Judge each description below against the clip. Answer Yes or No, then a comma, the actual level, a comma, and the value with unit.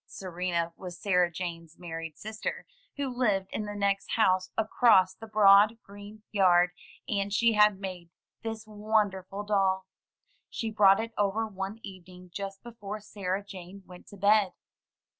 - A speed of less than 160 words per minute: Yes, average, 150 wpm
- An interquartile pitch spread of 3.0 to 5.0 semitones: No, narrow, 2.4 semitones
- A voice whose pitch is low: No, high, 200 Hz